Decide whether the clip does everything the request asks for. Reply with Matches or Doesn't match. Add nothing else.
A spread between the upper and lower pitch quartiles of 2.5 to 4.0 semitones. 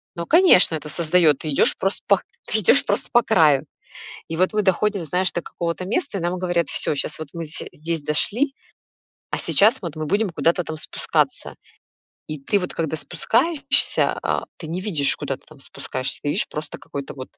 Doesn't match